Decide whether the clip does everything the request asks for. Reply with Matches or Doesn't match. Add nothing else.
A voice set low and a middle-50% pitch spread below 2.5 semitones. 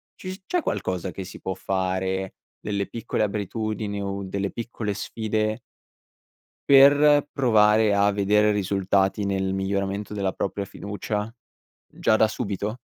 Matches